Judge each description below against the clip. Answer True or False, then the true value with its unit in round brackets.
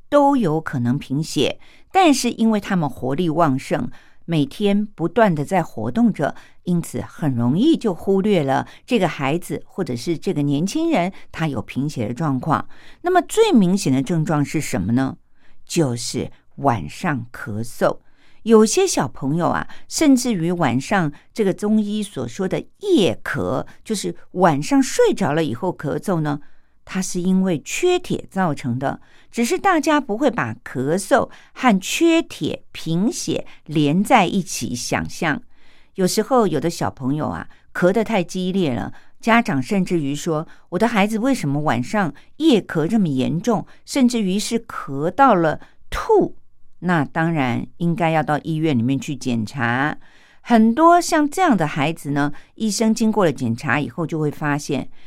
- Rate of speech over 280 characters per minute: False (230 characters per minute)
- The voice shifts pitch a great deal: True (7.8 semitones)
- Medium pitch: True (175 Hz)